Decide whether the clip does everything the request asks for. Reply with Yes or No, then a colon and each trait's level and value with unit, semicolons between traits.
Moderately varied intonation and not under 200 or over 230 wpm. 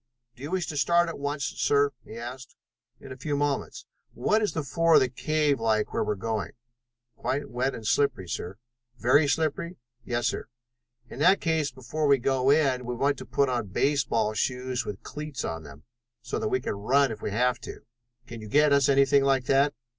Yes: average, 3.4 semitones; fast, 205 wpm